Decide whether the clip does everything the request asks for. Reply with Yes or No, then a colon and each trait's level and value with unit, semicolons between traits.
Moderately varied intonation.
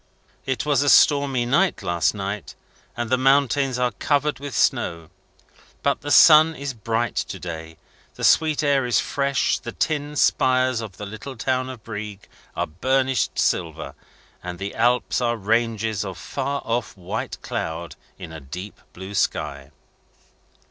No: wide, 5.7 semitones